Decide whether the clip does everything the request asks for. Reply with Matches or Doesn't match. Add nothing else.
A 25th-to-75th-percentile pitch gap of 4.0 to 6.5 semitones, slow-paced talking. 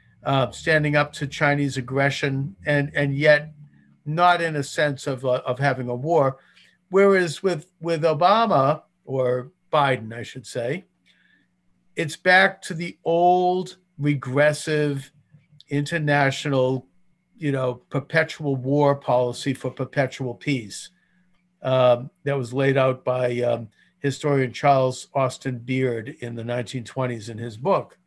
Doesn't match